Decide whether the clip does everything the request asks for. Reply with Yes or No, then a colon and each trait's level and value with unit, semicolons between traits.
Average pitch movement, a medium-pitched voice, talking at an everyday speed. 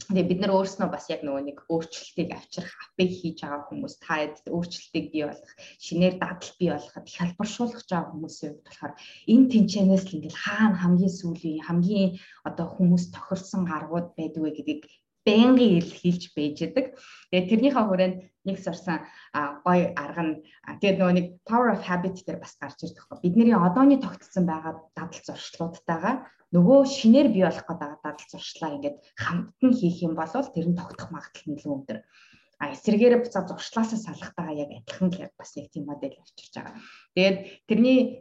Yes: average, 3.8 semitones; medium, 175 Hz; average, 170 wpm